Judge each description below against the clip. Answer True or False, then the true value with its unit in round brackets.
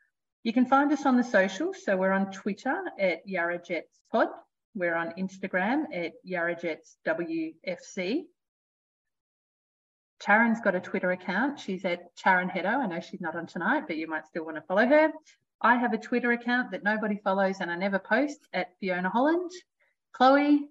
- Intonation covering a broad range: True (6.9 semitones)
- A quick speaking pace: False (175 wpm)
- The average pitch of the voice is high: True (200 Hz)